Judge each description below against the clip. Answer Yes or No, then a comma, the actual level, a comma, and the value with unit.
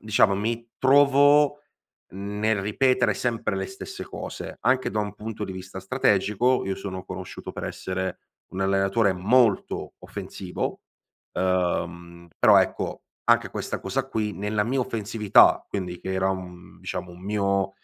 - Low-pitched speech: Yes, low, 100 Hz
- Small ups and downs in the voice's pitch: No, average, 3.7 semitones